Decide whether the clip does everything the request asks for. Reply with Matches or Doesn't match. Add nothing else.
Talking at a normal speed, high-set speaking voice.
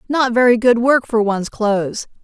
Matches